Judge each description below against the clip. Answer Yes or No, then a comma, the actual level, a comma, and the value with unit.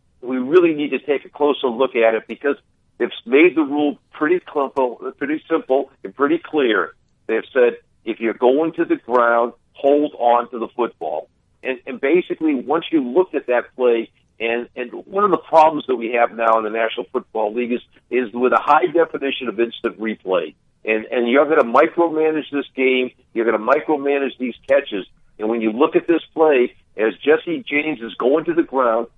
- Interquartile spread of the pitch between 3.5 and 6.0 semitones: Yes, average, 5.2 semitones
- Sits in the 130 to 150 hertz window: Yes, low, 135 Hz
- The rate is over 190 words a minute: Yes, average, 200 wpm